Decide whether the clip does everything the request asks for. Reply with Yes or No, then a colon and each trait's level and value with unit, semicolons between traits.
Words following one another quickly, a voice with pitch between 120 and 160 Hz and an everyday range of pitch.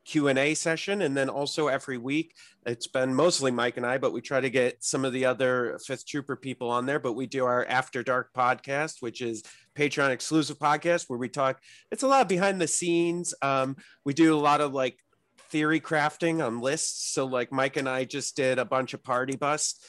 Yes: fast, 225 wpm; low, 135 Hz; average, 3.0 semitones